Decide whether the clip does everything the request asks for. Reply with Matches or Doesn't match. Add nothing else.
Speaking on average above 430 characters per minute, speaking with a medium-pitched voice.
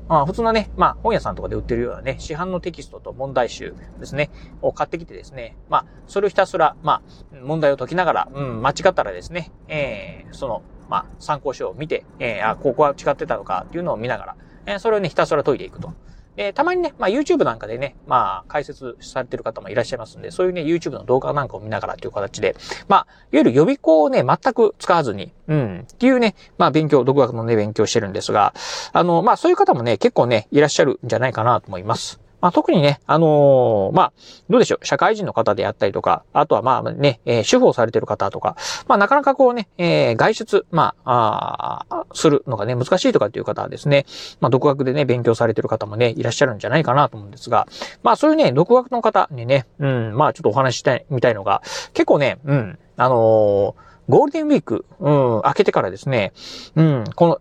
Matches